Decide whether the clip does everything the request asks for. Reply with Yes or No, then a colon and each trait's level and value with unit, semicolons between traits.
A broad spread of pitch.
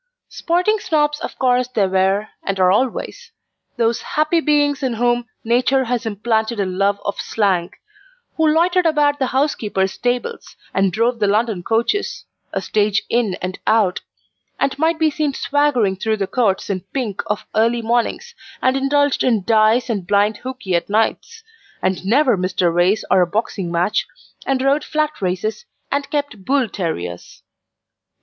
Yes: wide, 6.1 semitones